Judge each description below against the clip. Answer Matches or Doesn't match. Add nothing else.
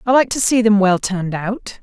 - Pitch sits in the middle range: Doesn't match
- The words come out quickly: Matches